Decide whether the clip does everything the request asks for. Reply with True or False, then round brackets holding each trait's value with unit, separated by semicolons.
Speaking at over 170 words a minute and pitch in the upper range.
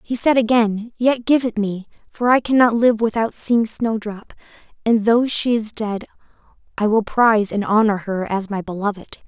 True (180 wpm; 220 Hz)